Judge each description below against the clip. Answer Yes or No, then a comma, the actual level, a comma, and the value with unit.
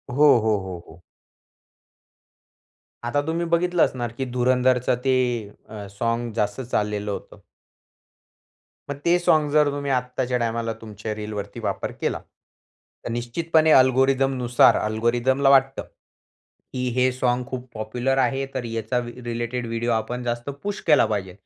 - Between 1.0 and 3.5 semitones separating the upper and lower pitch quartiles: Yes, average, 2.8 semitones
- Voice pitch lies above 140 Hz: No, low, 125 Hz